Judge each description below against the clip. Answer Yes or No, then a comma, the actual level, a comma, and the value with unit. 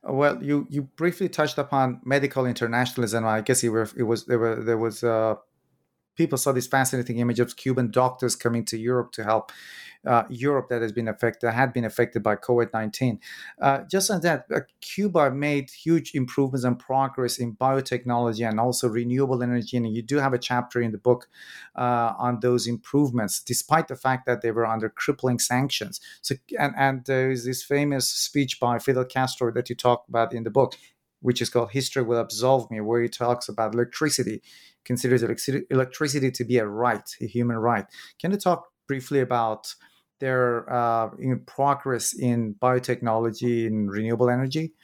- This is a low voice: Yes, low, 125 Hz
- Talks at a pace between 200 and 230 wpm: No, average, 180 wpm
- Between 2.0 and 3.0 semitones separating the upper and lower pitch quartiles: Yes, narrow, 2.4 semitones